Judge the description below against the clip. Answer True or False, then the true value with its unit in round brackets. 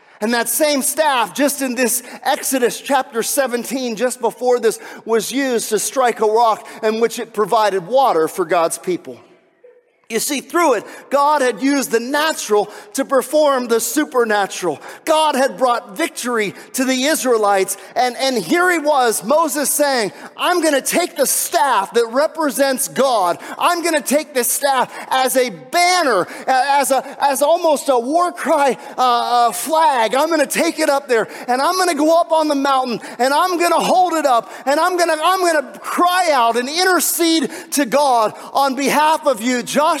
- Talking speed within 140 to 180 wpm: True (175 wpm)